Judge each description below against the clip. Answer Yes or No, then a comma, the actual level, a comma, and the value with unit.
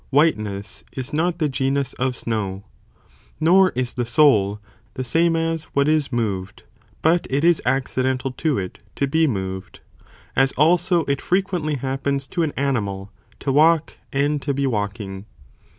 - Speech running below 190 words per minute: Yes, average, 150 wpm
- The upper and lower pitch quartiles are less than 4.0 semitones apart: No, wide, 5.5 semitones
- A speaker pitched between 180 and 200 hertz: No, low, 135 Hz